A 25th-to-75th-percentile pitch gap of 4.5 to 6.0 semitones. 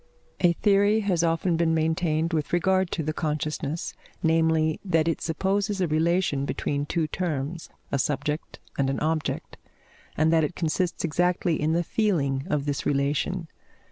No: average, 2.7 semitones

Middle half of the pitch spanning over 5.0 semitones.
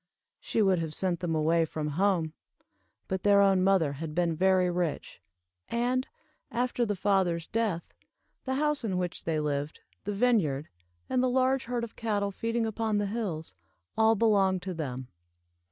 Yes: wide, 5.4 semitones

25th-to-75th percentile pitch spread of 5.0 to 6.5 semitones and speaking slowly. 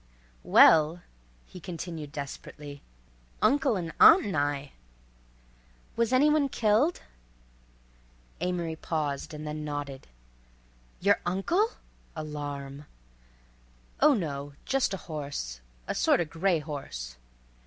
Yes: average, 5.3 semitones; slow, 95 wpm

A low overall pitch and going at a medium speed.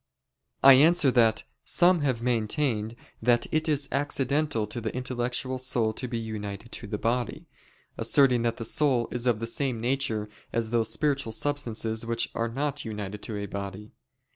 Yes: low, 120 Hz; average, 165 wpm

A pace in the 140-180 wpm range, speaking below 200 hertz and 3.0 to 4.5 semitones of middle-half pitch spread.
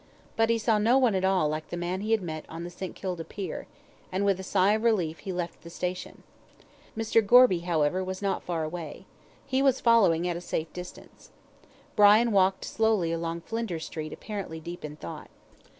No: average, 200 wpm; medium, 185 Hz; average, 4.2 semitones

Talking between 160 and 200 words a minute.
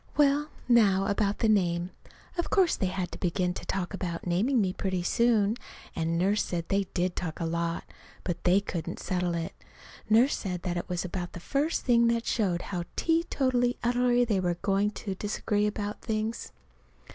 Yes: average, 180 wpm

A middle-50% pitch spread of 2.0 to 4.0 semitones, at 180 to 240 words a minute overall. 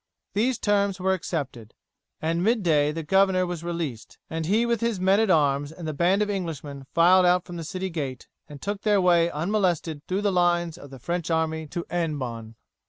Yes: average, 3.6 semitones; average, 200 wpm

